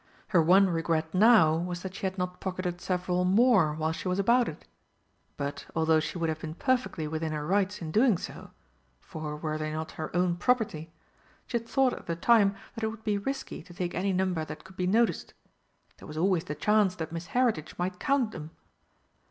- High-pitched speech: No, medium, 180 Hz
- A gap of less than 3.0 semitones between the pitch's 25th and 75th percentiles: No, average, 4.3 semitones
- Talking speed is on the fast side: Yes, fast, 210 wpm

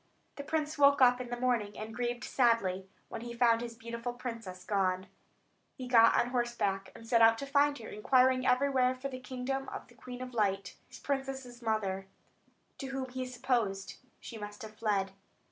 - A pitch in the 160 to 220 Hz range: No, high, 240 Hz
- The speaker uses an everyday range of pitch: Yes, average, 3.0 semitones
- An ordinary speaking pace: Yes, average, 190 wpm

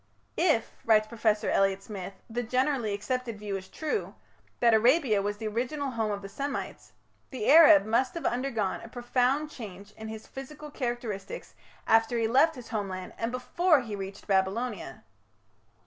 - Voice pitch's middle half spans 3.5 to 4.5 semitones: Yes, average, 3.9 semitones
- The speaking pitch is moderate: No, high, 230 Hz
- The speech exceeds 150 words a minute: Yes, average, 160 wpm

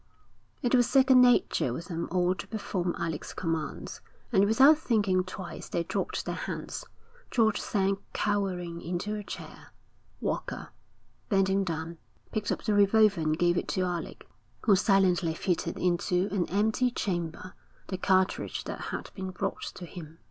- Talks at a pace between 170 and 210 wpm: No, average, 155 wpm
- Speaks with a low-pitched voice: No, high, 190 Hz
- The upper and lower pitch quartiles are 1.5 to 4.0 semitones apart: Yes, average, 3.1 semitones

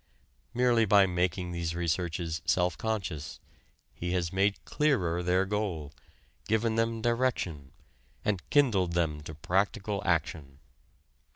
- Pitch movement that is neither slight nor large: Yes, average, 4.5 semitones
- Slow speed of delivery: Yes, slow, 115 wpm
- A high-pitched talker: No, very low, 90 Hz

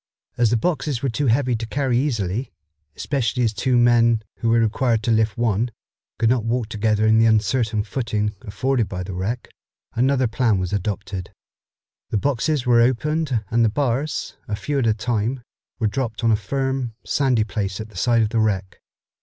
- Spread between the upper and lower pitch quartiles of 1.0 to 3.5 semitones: Yes, average, 2.9 semitones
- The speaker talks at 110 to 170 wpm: No, average, 185 wpm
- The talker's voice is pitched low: Yes, low, 115 Hz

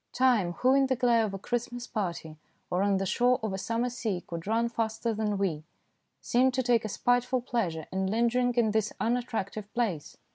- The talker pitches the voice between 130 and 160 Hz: No, high, 225 Hz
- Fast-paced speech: No, average, 195 wpm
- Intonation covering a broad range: No, average, 3.9 semitones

